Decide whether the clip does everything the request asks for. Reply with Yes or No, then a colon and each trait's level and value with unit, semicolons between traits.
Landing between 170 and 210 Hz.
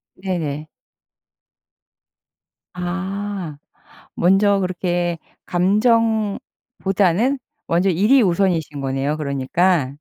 Yes: medium, 185 Hz